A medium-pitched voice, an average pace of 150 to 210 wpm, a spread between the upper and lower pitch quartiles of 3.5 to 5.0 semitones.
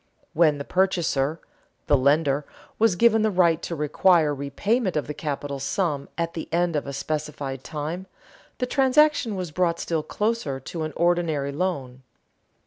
Yes: medium, 160 Hz; average, 155 wpm; average, 4.4 semitones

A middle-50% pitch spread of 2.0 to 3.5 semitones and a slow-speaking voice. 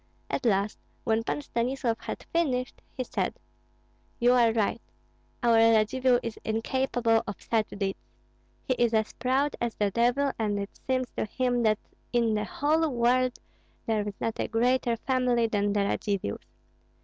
No: average, 2.7 semitones; average, 160 wpm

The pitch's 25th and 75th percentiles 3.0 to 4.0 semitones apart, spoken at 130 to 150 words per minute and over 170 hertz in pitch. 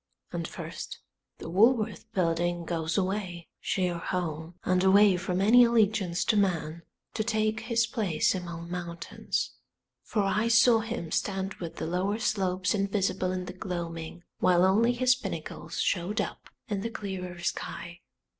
Yes: average, 3.7 semitones; average, 145 wpm; high, 190 Hz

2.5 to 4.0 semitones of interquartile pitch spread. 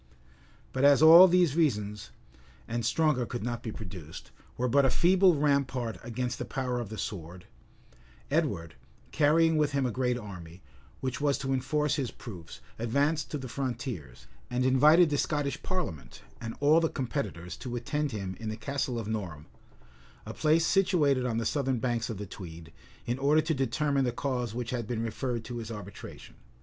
No: average, 4.7 semitones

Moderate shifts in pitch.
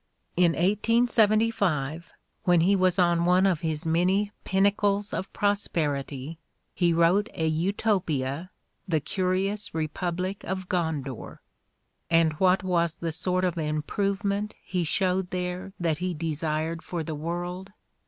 Yes: average, 3.1 semitones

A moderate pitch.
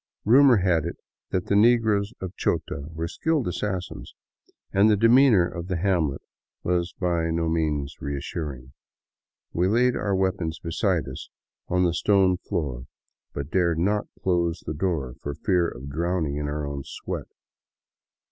No: very low, 85 Hz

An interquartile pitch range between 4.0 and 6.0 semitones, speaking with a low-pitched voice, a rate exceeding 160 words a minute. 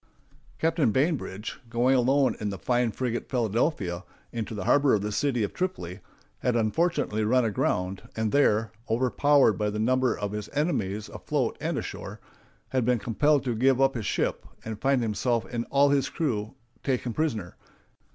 Yes: average, 4.3 semitones; low, 120 Hz; average, 170 wpm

